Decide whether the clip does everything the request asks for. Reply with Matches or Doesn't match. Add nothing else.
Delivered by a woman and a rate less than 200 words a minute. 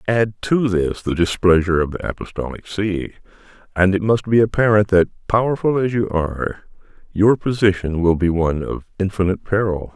Doesn't match